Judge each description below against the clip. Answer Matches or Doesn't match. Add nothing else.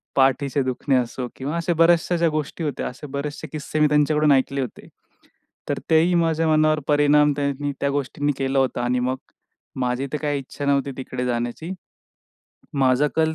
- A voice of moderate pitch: Matches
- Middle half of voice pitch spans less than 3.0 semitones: Matches